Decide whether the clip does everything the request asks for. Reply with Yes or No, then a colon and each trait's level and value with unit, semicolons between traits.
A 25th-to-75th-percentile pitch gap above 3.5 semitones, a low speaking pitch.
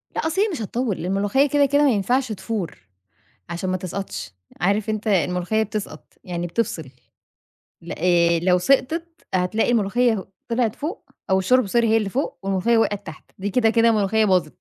No: average, 4.7 semitones; high, 210 Hz